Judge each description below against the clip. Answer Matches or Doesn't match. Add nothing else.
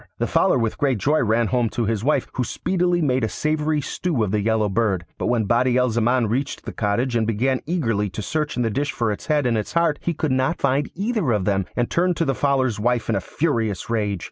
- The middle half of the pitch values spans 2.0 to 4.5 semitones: Doesn't match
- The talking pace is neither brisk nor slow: Doesn't match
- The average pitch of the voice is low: Matches